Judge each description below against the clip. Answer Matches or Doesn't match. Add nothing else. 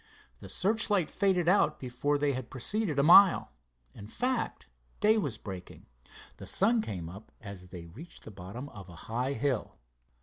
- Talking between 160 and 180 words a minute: Matches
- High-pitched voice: Doesn't match